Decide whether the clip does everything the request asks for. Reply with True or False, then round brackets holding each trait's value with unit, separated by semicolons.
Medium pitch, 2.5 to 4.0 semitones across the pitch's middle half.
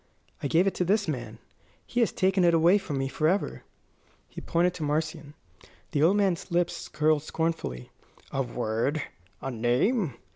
False (160 Hz; 4.8 semitones)